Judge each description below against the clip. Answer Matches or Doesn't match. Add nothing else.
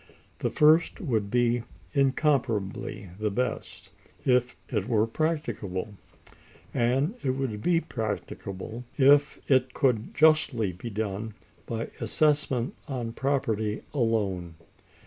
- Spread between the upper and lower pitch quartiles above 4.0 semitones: Matches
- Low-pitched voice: Matches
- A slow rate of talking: Matches